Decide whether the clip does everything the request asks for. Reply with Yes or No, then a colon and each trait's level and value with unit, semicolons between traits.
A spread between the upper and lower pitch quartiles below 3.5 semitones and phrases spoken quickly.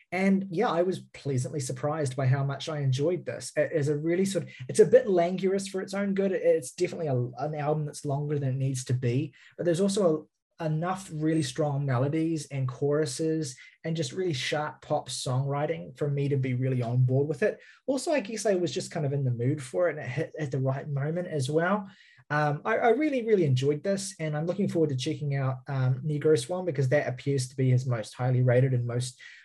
No: average, 4.4 semitones; fast, 230 wpm